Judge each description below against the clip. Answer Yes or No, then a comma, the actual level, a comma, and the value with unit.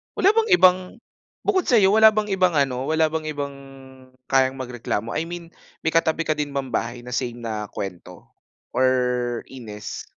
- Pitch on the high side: No, medium, 140 Hz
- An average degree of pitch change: No, wide, 5.8 semitones